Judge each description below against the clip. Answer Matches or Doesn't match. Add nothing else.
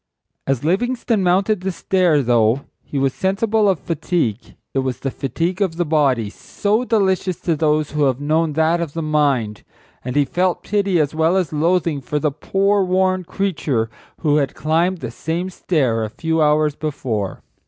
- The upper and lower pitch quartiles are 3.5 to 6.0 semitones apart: Matches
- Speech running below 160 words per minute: Doesn't match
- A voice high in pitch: Doesn't match